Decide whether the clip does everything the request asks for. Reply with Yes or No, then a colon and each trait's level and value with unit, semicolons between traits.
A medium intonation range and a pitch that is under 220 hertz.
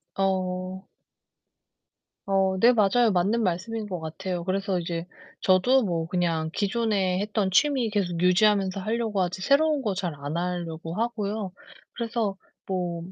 Yes: average, 3.4 semitones; high, 190 Hz